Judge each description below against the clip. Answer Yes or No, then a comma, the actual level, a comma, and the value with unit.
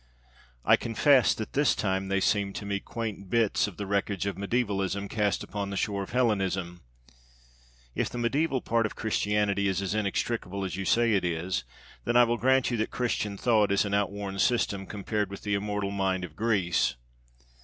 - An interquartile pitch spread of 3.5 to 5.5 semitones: No, average, 2.7 semitones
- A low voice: Yes, low, 100 Hz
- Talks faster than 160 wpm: Yes, average, 185 wpm